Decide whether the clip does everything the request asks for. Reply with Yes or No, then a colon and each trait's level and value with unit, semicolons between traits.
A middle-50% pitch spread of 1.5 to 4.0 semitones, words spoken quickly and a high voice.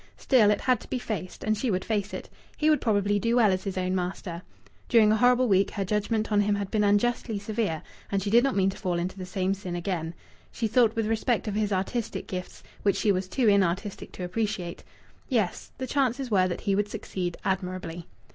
Yes: average, 3.3 semitones; fast, 225 wpm; high, 205 Hz